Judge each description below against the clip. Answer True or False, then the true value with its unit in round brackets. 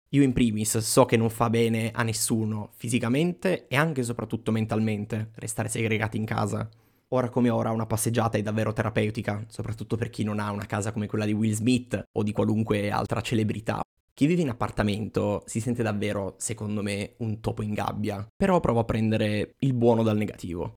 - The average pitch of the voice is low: True (110 Hz)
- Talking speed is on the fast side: True (190 wpm)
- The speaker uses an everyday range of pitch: False (1.9 semitones)